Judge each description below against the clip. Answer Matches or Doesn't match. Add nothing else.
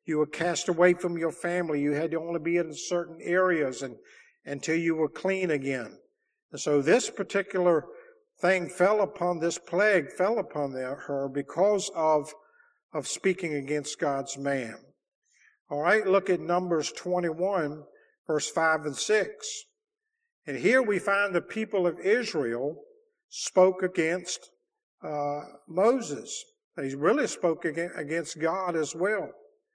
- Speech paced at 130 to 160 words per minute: Matches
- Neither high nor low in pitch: Matches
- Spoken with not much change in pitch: Doesn't match